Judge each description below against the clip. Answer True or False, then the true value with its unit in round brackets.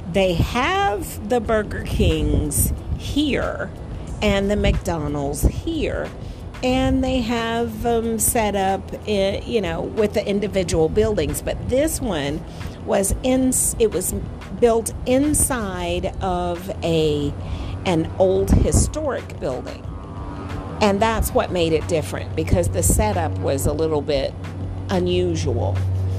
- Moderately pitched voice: True (175 Hz)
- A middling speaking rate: False (120 wpm)